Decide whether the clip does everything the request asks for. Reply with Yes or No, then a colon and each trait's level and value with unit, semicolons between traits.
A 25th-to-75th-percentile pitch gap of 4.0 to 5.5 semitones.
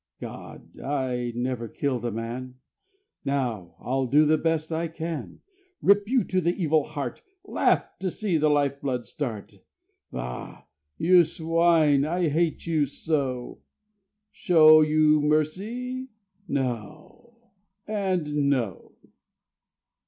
Yes: average, 4.5 semitones